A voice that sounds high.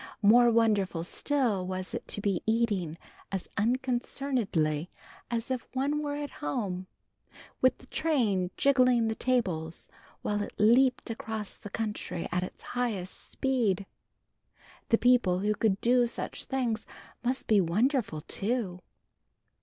Yes: high, 220 Hz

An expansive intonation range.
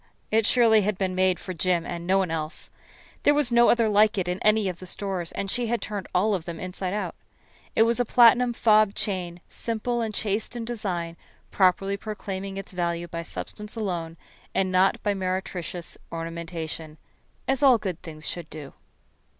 No: average, 3.9 semitones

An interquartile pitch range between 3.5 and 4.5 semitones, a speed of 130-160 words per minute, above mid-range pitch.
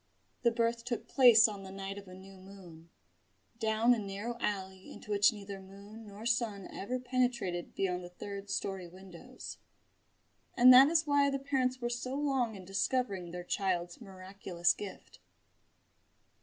Yes: average, 4.2 semitones; average, 155 wpm; high, 205 Hz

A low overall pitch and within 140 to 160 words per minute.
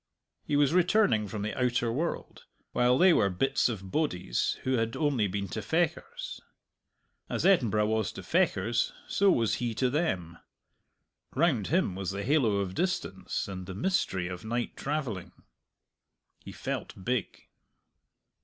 Yes: low, 120 Hz; average, 145 wpm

